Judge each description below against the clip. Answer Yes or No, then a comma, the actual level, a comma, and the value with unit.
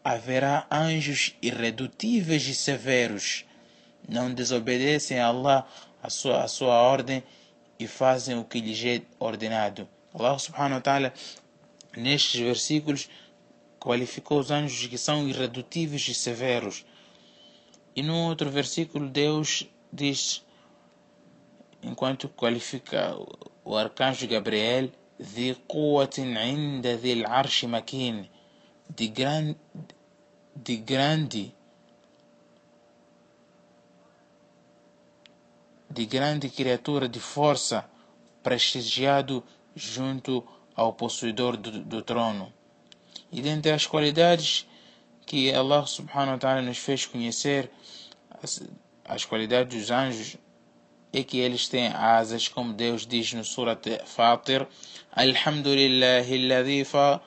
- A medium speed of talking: No, slow, 100 wpm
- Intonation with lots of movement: No, average, 3.0 semitones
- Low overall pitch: Yes, low, 130 Hz